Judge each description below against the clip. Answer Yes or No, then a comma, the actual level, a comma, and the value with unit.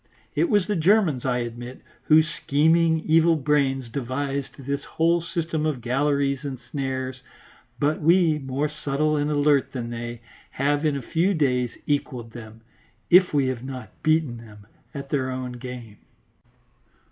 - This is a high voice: No, medium, 140 Hz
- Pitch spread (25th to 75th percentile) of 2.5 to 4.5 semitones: Yes, average, 3.4 semitones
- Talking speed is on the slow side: No, average, 150 wpm